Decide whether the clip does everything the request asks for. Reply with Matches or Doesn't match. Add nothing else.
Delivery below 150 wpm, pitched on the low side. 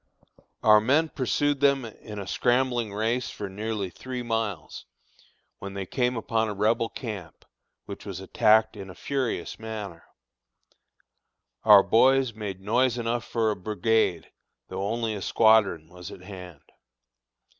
Matches